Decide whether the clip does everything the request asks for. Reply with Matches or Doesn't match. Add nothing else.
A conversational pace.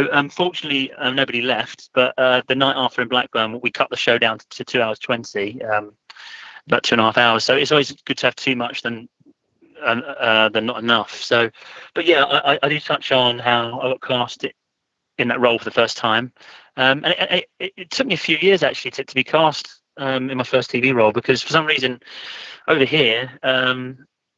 Doesn't match